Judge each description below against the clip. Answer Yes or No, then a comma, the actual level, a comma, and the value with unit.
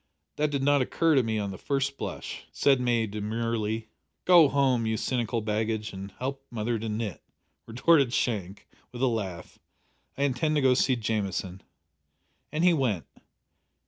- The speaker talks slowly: No, average, 165 wpm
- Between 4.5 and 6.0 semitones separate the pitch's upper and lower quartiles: No, average, 4.1 semitones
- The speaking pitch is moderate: No, low, 115 Hz